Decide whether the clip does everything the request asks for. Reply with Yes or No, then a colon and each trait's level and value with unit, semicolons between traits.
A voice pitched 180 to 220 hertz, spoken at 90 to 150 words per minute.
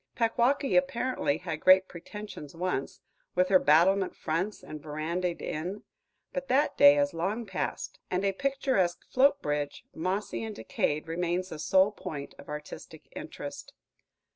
Yes: medium, 185 Hz; average, 140 wpm